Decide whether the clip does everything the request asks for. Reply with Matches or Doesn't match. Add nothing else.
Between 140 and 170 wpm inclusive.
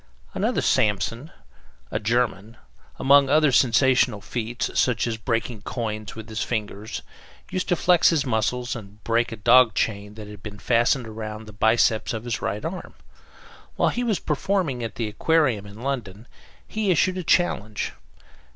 Matches